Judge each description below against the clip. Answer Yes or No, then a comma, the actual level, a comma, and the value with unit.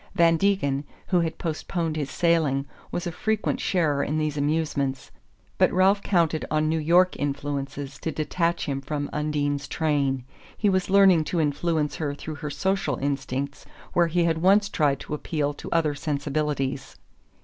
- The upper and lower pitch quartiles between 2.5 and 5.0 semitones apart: Yes, average, 3.0 semitones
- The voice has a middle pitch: Yes, medium, 155 Hz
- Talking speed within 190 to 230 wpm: No, average, 160 wpm